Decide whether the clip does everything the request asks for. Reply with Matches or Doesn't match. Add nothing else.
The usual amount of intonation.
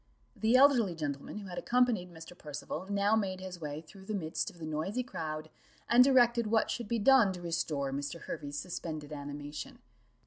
Doesn't match